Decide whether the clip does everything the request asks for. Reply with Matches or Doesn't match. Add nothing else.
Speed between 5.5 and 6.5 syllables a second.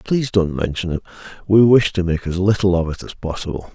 Matches